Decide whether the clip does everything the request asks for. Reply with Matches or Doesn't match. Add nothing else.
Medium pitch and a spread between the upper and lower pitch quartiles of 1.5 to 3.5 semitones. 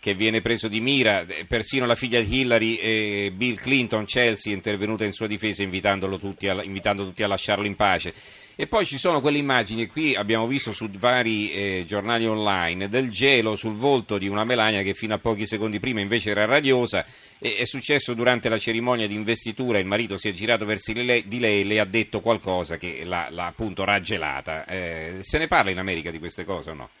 Doesn't match